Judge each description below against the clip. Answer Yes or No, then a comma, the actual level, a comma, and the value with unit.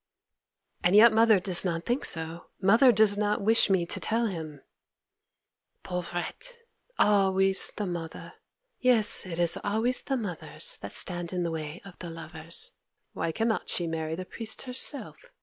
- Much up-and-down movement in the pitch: No, average, 4.6 semitones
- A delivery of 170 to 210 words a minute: No, average, 155 wpm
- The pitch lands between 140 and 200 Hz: Yes, high, 190 Hz